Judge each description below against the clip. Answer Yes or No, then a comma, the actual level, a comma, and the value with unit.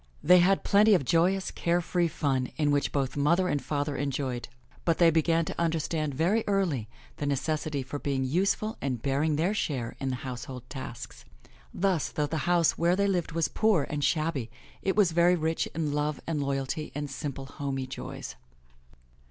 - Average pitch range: Yes, average, 3.8 semitones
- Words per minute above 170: Yes, average, 180 wpm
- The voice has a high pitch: No, medium, 155 Hz